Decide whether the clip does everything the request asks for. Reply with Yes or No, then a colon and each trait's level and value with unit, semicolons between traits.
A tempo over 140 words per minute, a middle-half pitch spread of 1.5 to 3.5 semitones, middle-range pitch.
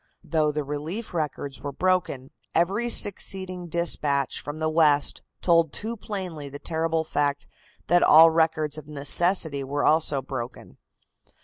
No: slow, 135 wpm; average, 3.2 semitones; medium, 155 Hz